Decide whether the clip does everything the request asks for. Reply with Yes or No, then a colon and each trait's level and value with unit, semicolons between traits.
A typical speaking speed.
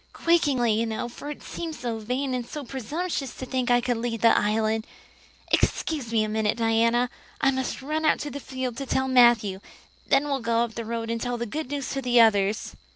No: fast, 220 wpm